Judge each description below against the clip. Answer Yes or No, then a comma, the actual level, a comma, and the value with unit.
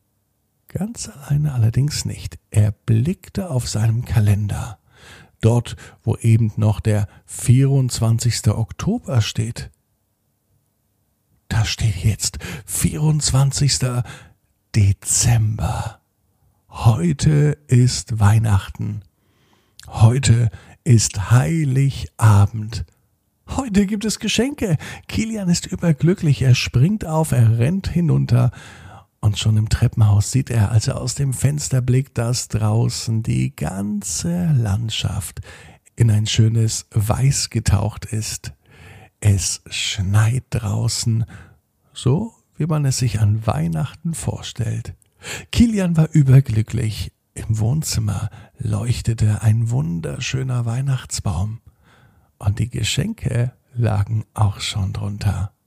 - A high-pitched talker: No, low, 115 Hz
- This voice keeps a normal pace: No, slow, 100 wpm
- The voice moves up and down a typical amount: Yes, average, 3.8 semitones